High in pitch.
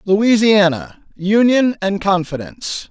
Yes: high, 200 Hz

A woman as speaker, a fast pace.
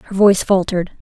No: female; average, 165 wpm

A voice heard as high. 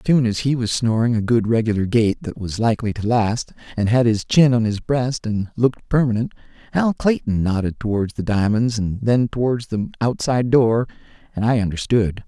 No: low, 115 Hz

